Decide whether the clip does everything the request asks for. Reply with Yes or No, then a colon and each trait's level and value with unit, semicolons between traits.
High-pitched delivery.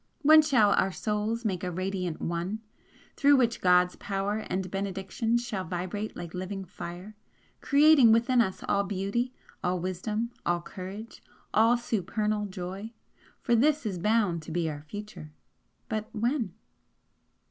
Yes: high, 205 Hz